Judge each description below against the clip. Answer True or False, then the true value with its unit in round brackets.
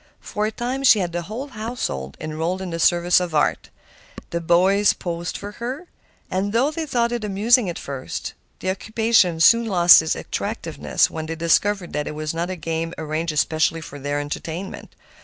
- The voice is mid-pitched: True (180 Hz)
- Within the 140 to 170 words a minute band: False (180 wpm)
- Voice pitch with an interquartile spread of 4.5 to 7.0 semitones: True (5.0 semitones)